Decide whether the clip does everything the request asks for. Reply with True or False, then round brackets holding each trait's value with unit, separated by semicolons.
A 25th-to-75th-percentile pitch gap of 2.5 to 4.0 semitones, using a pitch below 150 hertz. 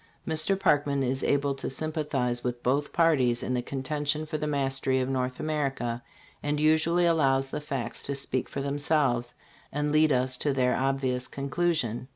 True (2.8 semitones; 140 Hz)